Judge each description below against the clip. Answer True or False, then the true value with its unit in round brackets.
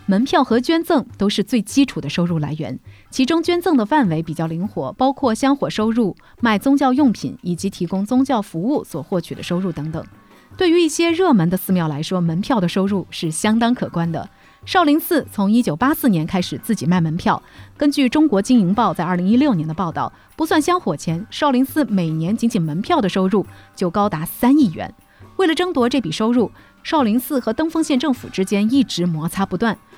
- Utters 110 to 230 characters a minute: False (310 characters per minute)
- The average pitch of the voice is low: False (215 Hz)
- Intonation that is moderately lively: False (7.4 semitones)